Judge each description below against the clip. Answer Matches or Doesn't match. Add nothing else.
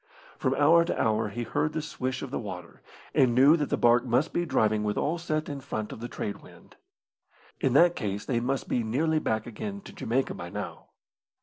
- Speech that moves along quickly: Matches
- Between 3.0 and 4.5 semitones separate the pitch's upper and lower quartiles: Doesn't match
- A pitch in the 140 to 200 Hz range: Doesn't match